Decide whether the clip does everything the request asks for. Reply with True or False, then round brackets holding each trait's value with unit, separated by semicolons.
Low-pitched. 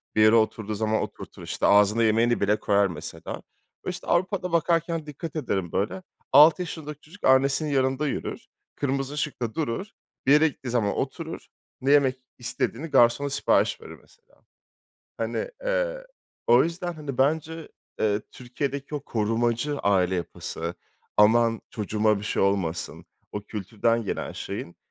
True (130 Hz)